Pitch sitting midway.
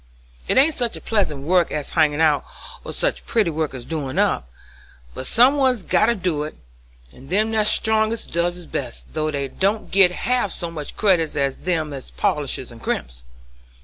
Yes: medium, 170 Hz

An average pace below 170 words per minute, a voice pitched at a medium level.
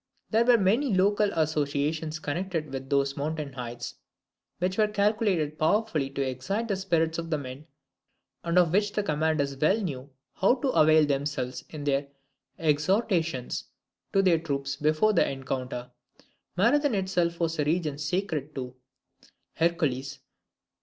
Yes: average, 140 wpm; medium, 155 Hz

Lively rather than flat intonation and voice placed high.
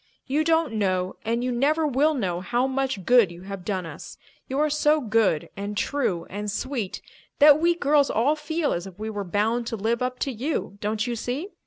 Yes: wide, 6.0 semitones; high, 240 Hz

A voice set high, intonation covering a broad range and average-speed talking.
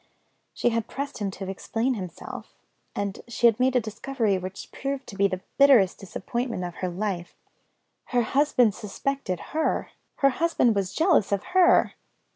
Yes: high, 225 Hz; wide, 5.7 semitones; average, 160 wpm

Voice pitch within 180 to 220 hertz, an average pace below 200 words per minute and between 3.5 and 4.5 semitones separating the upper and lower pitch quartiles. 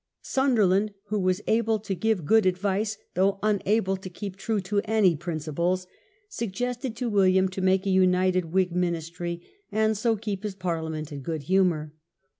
No: high, 190 Hz; average, 160 wpm; average, 3.0 semitones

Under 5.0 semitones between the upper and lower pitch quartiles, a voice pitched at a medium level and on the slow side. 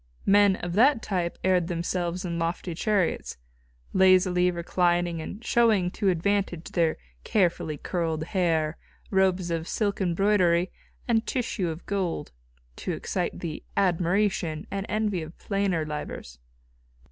Yes: average, 2.8 semitones; medium, 180 Hz; slow, 125 wpm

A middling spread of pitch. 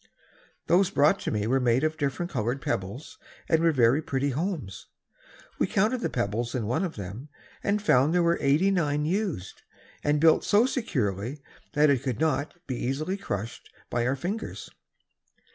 No: wide, 6.0 semitones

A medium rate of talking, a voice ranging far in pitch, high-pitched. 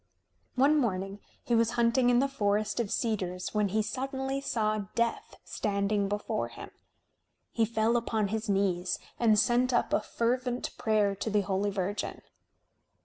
No: average, 150 wpm; average, 3.0 semitones; high, 220 Hz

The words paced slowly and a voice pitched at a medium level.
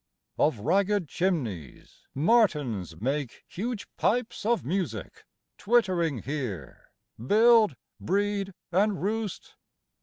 Yes: slow, 95 wpm; medium, 180 Hz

